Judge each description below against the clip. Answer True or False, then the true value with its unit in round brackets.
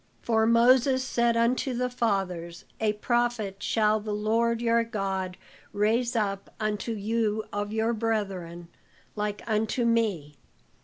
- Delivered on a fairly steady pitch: True (2.3 semitones)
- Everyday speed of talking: False (125 wpm)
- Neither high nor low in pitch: False (220 Hz)